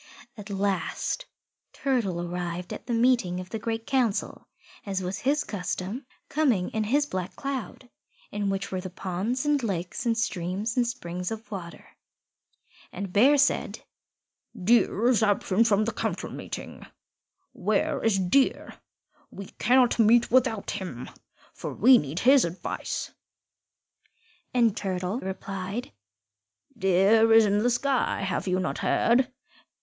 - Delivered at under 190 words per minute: Yes, slow, 135 wpm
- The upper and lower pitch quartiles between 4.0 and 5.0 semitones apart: Yes, average, 4.6 semitones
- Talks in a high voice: Yes, high, 210 Hz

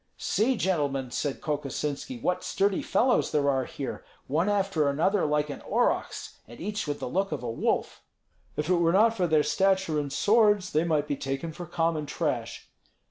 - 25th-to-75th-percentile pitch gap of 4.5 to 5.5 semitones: Yes, average, 5.0 semitones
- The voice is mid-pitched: Yes, medium, 160 Hz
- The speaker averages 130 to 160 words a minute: No, average, 185 wpm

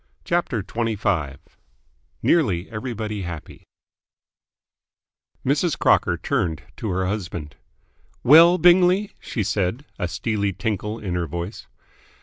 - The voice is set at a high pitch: No, low, 105 Hz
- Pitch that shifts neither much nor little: No, wide, 6.4 semitones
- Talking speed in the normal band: No, slow, 105 wpm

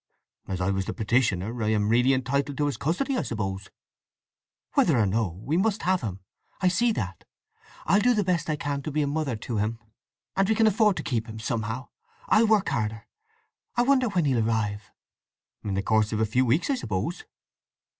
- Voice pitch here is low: Yes, low, 125 Hz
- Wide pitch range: Yes, wide, 8.8 semitones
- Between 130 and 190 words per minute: No, fast, 205 wpm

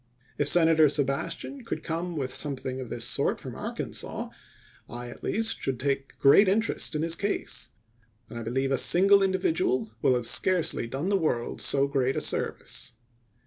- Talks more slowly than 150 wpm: No, average, 170 wpm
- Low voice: No, medium, 150 Hz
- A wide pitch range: Yes, wide, 6.2 semitones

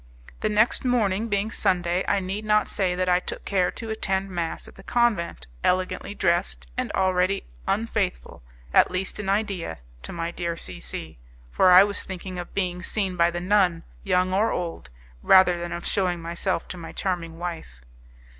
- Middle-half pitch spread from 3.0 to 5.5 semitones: No, narrow, 2.4 semitones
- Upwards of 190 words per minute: No, average, 180 wpm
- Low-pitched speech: No, medium, 185 Hz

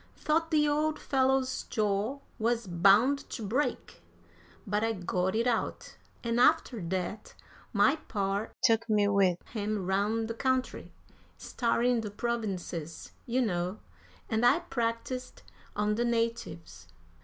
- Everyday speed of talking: No, slow, 130 wpm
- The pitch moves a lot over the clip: No, average, 3.8 semitones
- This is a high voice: Yes, high, 225 Hz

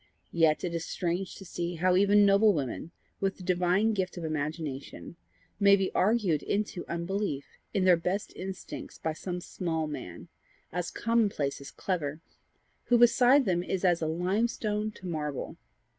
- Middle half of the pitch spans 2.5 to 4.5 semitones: Yes, average, 3.6 semitones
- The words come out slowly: No, average, 160 wpm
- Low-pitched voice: No, medium, 180 Hz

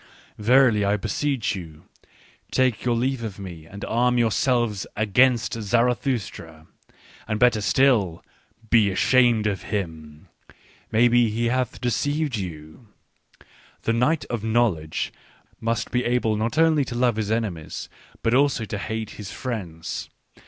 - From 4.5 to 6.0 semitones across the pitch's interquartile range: No, average, 3.5 semitones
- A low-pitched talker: Yes, low, 115 Hz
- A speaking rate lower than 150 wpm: Yes, average, 140 wpm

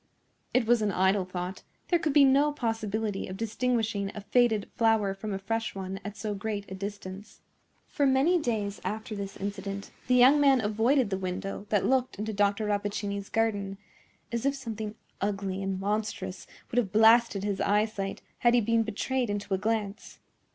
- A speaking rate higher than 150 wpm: Yes, average, 175 wpm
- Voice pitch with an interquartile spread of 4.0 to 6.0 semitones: No, average, 2.7 semitones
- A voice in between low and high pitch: No, high, 210 Hz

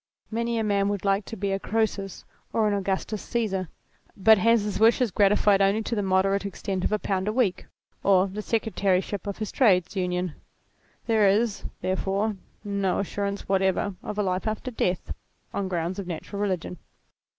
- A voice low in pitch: No, high, 200 Hz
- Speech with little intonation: Yes, narrow, 2.0 semitones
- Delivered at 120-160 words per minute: No, average, 175 wpm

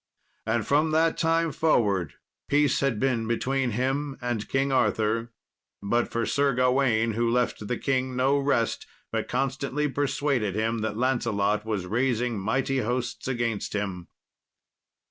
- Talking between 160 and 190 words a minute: No, average, 140 wpm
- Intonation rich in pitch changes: No, average, 3.6 semitones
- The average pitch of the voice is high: No, low, 125 Hz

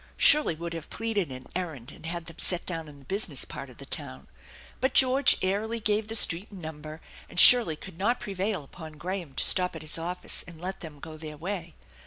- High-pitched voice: No, medium, 175 Hz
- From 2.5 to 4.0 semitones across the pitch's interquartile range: No, average, 4.4 semitones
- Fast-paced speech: Yes, fast, 220 wpm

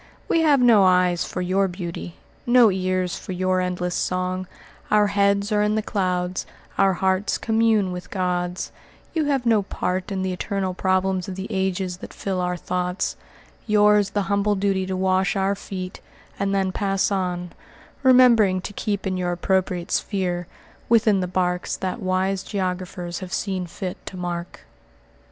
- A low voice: No, high, 190 Hz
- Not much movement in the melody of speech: Yes, narrow, 1.8 semitones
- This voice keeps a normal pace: Yes, average, 165 wpm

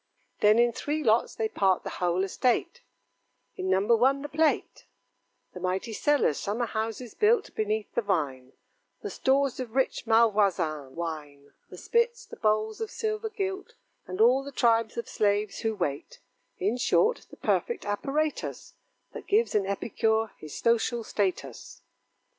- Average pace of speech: Yes, average, 150 wpm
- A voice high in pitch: Yes, high, 220 Hz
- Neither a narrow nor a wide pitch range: No, wide, 5.9 semitones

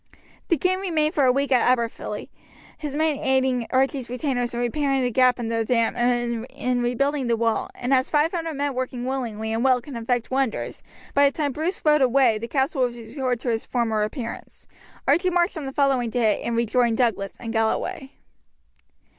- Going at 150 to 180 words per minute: No, average, 190 wpm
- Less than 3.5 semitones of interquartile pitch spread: Yes, average, 3.0 semitones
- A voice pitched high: Yes, very high, 255 Hz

